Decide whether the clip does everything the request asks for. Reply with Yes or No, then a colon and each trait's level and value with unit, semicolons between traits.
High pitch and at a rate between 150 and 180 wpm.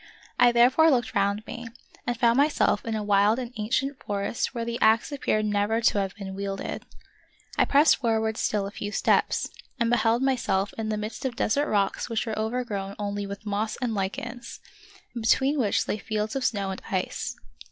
No: high, 220 Hz; average, 190 wpm